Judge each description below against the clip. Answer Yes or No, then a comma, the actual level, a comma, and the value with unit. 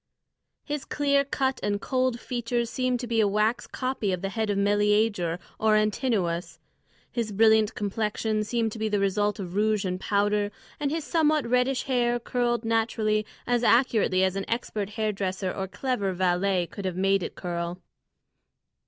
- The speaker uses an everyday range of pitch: Yes, average, 3.4 semitones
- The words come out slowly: No, average, 165 wpm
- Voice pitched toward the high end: Yes, high, 215 Hz